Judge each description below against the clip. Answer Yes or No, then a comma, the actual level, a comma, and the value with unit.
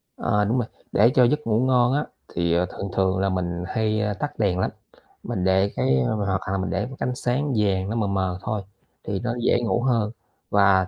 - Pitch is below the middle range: Yes, low, 100 Hz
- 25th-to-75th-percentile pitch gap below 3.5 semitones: No, average, 3.8 semitones